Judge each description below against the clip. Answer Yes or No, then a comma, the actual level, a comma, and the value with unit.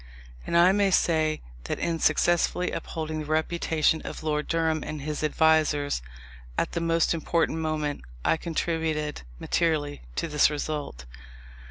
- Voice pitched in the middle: Yes, medium, 155 Hz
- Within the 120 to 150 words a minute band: Yes, average, 140 wpm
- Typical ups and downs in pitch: No, narrow, 1.6 semitones